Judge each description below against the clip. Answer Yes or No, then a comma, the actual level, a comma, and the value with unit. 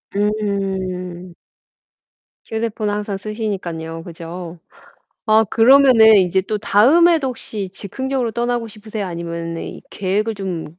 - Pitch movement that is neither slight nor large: Yes, average, 3.6 semitones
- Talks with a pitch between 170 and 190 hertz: No, high, 205 Hz